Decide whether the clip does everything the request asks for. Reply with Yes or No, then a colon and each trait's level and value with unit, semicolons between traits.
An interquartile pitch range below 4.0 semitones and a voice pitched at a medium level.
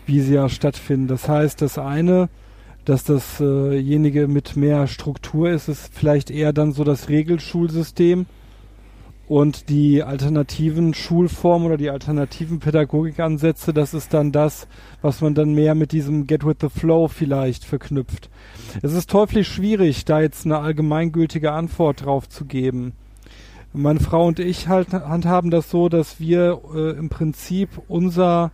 Yes: average, 2.7 semitones; medium, 150 Hz